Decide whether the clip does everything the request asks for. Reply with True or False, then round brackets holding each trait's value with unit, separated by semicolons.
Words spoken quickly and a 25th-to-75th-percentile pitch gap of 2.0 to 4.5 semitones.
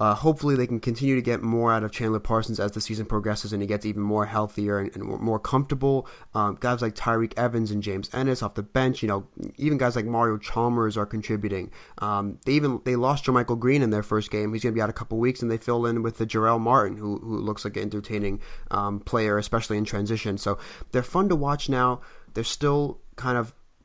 True (240 wpm; 2.8 semitones)